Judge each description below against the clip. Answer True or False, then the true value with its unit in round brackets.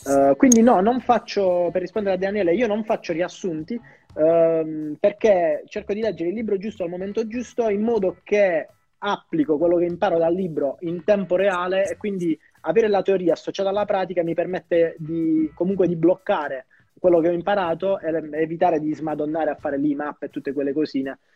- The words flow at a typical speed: False (185 wpm)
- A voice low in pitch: False (180 Hz)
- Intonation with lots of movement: False (4.2 semitones)